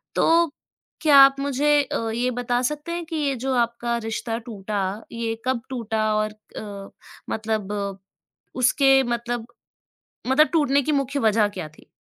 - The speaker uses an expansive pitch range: No, average, 3.9 semitones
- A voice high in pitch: Yes, high, 240 Hz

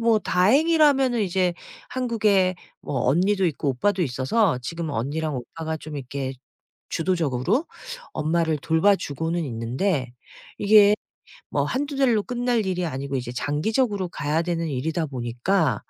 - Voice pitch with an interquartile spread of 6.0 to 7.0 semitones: Yes, wide, 6.6 semitones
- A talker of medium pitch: Yes, medium, 170 Hz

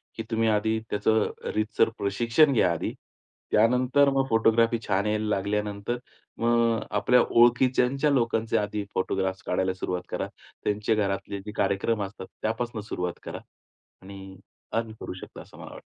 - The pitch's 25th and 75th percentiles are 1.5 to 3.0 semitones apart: Yes, average, 2.7 semitones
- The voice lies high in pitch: No, low, 110 Hz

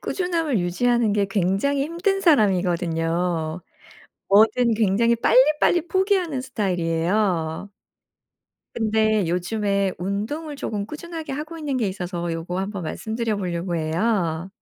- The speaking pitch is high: Yes, high, 210 Hz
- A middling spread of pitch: No, wide, 6.8 semitones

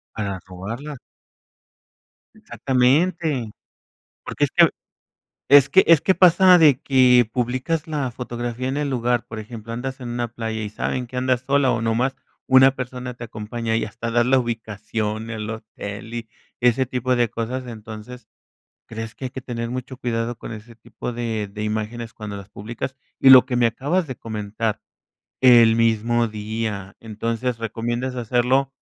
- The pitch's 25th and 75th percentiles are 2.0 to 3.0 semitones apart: Yes, narrow, 2.4 semitones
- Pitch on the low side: Yes, low, 120 Hz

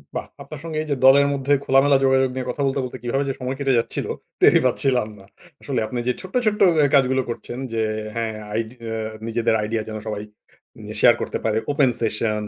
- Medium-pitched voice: No, low, 130 Hz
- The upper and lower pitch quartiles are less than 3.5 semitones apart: Yes, average, 3.1 semitones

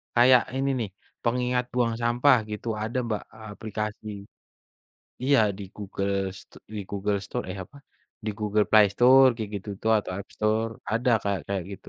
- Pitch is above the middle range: No, low, 110 Hz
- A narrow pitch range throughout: No, average, 3.1 semitones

